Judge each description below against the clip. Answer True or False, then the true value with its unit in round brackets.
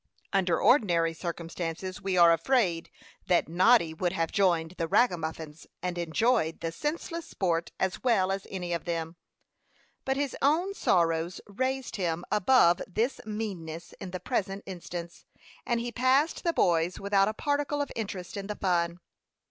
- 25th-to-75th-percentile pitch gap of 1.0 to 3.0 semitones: False (5.6 semitones)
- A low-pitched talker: False (185 Hz)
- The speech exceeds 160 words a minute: False (155 wpm)